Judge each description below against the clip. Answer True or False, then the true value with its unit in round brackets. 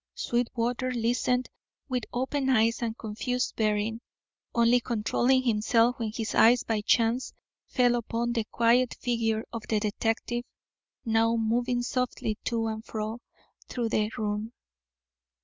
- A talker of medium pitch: False (230 Hz)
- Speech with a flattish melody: True (1.8 semitones)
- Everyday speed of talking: False (130 wpm)